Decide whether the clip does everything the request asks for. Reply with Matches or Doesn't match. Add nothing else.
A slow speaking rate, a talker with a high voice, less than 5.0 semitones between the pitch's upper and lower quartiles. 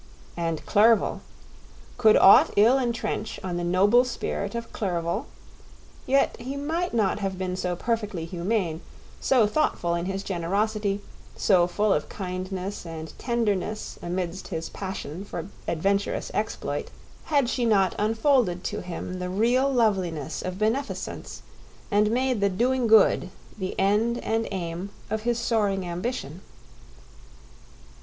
Matches